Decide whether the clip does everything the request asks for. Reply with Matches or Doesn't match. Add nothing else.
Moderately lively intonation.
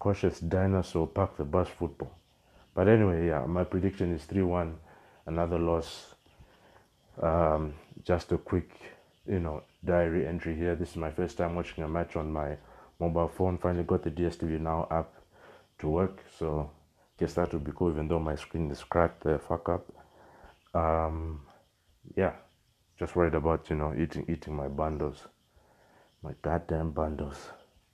Doesn't match